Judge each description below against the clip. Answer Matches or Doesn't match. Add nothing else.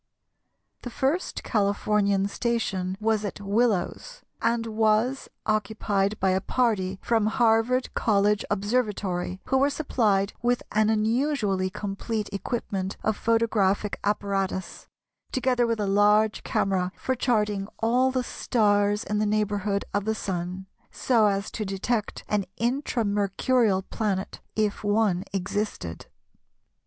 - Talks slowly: Matches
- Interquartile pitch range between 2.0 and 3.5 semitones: Matches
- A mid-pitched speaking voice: Doesn't match